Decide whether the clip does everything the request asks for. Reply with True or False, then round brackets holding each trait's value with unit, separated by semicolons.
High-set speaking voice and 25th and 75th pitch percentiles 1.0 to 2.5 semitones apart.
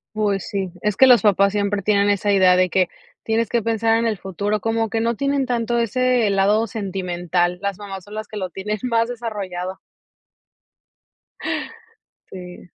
False (205 Hz; 2.9 semitones)